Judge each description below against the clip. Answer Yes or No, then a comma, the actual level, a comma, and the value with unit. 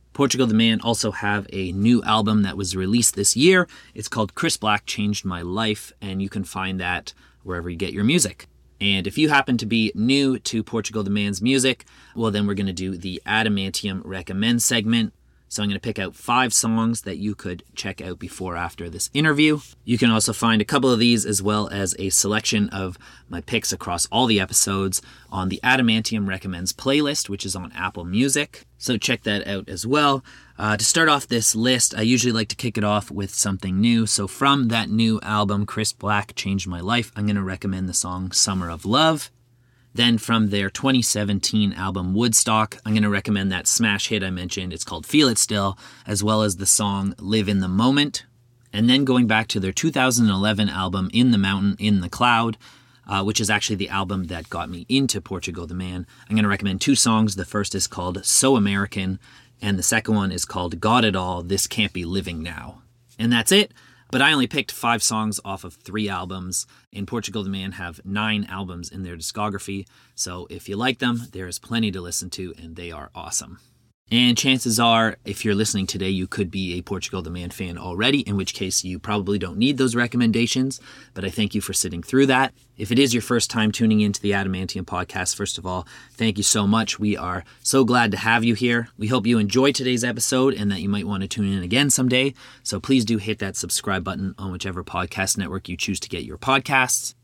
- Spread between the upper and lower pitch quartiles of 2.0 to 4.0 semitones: Yes, average, 3.6 semitones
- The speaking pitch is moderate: No, low, 105 Hz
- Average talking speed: No, fast, 215 wpm